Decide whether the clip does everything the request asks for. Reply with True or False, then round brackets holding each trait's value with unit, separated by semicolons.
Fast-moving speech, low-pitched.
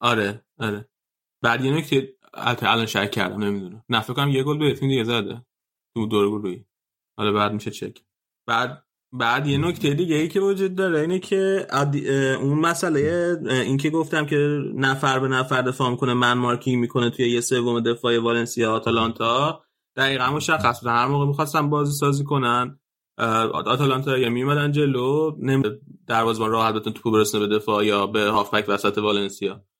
True (165 wpm; 125 Hz)